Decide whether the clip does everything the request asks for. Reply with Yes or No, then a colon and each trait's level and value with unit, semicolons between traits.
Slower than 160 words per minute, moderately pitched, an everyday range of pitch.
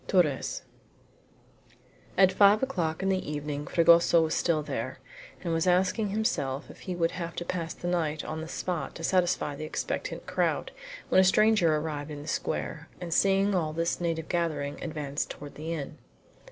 No: average, 175 wpm; medium, 165 Hz; average, 3.1 semitones